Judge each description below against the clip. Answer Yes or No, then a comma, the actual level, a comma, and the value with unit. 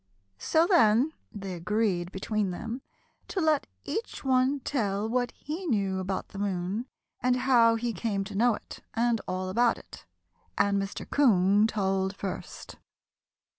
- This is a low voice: No, high, 215 Hz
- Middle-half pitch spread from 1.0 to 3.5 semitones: No, average, 4.2 semitones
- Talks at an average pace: Yes, average, 145 wpm